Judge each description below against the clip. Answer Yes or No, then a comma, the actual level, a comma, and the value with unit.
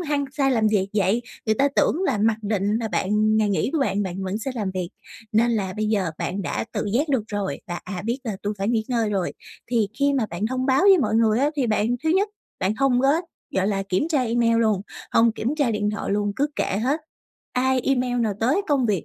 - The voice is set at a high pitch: Yes, high, 220 Hz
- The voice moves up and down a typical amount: Yes, average, 4.3 semitones